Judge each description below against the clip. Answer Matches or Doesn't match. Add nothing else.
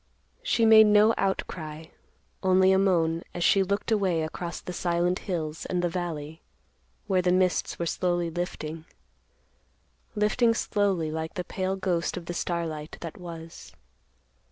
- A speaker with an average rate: Matches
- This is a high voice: Doesn't match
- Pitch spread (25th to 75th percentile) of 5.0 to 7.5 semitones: Doesn't match